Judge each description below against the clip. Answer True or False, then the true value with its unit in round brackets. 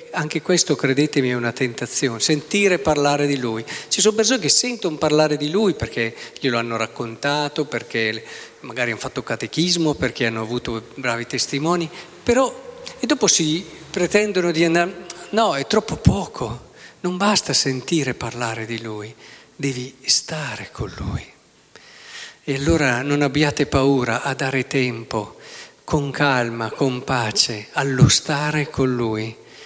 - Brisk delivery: False (140 wpm)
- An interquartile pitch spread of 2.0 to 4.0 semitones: False (5.5 semitones)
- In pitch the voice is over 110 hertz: True (140 Hz)